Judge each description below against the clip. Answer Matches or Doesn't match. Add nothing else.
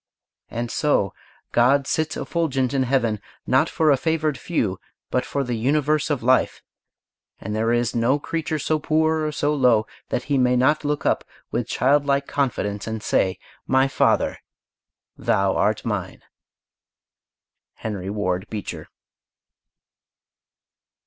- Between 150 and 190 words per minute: Doesn't match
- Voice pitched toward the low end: Matches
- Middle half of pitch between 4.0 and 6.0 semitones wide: Matches